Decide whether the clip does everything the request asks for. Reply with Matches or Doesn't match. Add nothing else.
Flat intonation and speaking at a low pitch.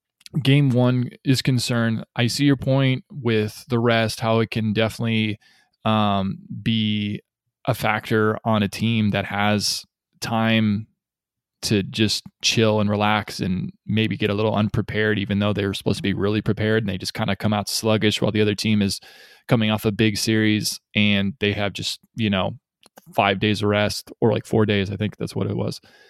Matches